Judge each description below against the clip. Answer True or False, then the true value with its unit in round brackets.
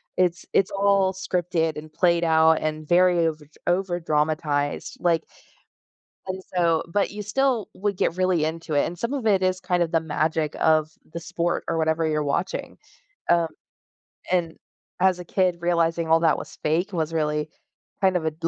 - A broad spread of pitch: False (2.6 semitones)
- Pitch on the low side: False (170 Hz)